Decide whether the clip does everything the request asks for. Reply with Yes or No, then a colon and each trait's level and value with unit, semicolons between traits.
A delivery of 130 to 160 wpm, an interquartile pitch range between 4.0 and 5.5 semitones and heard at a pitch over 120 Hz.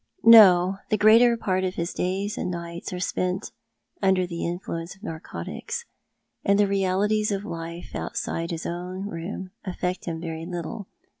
No: average, 155 wpm; average, 2.7 semitones; medium, 185 Hz